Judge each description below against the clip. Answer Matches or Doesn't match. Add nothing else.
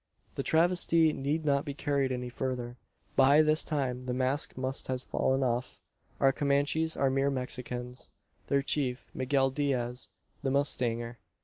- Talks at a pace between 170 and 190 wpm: Doesn't match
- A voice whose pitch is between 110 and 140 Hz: Matches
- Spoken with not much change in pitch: Matches